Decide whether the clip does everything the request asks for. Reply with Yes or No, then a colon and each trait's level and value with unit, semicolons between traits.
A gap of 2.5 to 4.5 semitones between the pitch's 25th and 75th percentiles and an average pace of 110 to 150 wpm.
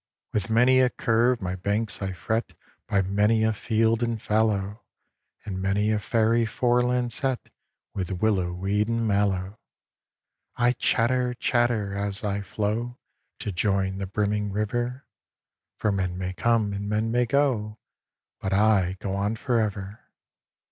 Yes: average, 2.9 semitones; average, 145 wpm